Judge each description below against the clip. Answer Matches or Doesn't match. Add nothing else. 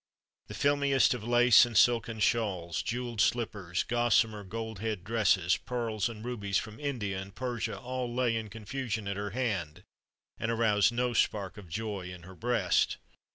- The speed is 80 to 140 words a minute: Doesn't match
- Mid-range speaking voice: Doesn't match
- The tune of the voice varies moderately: Matches